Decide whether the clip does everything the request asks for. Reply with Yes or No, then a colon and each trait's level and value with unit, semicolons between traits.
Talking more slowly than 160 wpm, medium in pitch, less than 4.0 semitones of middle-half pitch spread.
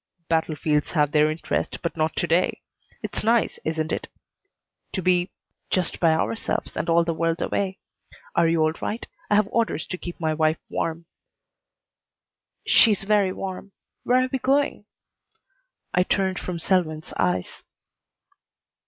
Yes: average, 145 wpm; medium, 170 Hz; average, 3.5 semitones